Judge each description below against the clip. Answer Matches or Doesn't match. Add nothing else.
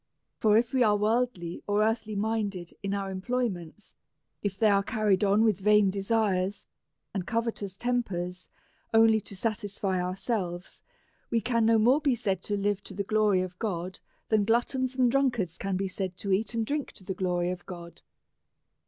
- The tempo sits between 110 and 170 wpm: Doesn't match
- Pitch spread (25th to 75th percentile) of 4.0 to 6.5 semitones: Doesn't match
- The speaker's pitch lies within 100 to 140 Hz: Doesn't match